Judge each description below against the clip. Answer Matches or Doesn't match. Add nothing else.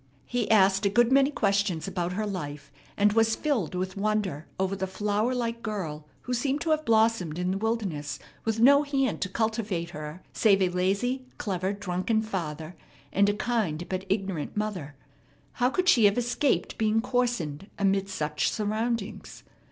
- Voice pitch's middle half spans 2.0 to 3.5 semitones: Doesn't match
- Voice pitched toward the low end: Doesn't match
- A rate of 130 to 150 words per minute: Doesn't match